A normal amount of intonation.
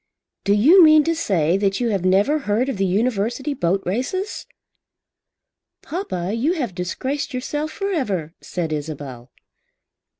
No: wide, 8.2 semitones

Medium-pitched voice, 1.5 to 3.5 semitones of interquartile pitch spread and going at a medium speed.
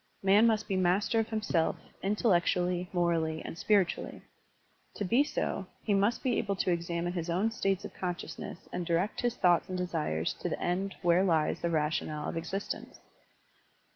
Yes: medium, 180 Hz; average, 2.8 semitones; average, 170 wpm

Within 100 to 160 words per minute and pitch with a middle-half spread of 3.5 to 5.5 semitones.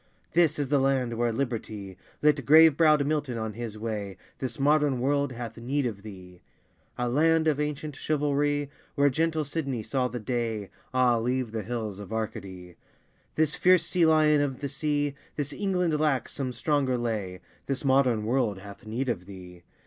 No: average, 170 wpm; average, 4.7 semitones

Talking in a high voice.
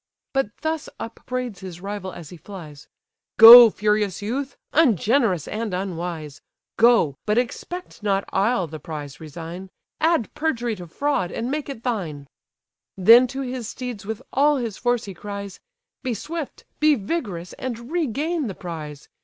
Yes: high, 215 Hz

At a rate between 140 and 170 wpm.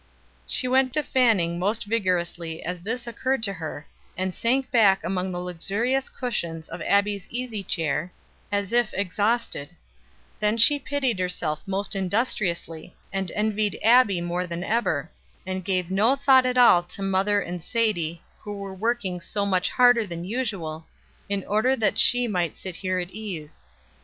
Yes: average, 160 wpm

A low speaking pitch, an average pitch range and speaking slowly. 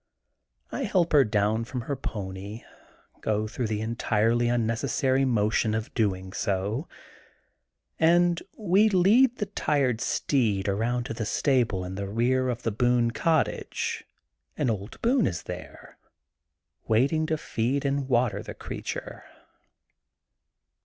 Yes: low, 120 Hz; average, 4.8 semitones; slow, 130 wpm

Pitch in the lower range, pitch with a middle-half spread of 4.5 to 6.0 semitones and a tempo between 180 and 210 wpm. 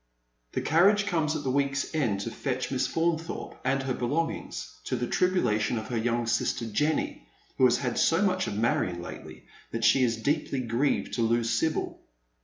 Yes: low, 130 Hz; average, 5.3 semitones; average, 185 wpm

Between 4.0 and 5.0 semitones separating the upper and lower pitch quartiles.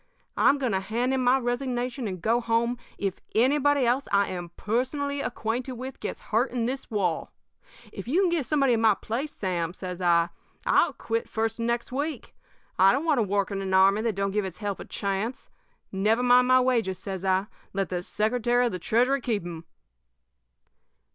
Yes: average, 4.5 semitones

